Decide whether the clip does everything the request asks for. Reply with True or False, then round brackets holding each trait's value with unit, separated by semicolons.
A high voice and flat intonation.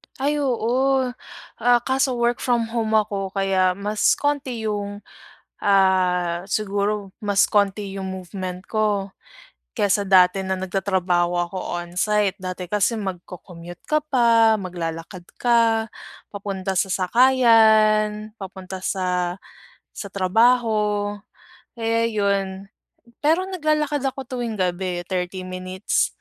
False (200 Hz; 3.6 semitones)